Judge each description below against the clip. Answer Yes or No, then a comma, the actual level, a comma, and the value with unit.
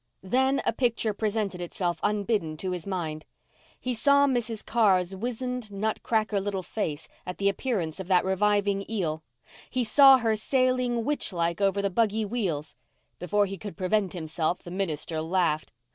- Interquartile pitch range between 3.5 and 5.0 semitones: Yes, average, 4.2 semitones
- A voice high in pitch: Yes, high, 200 Hz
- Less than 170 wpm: Yes, average, 160 wpm